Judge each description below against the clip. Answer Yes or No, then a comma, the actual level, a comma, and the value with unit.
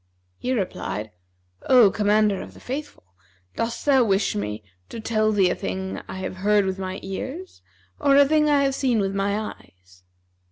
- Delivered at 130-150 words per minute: No, average, 175 wpm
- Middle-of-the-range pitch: No, high, 210 Hz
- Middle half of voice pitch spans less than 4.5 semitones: No, wide, 5.4 semitones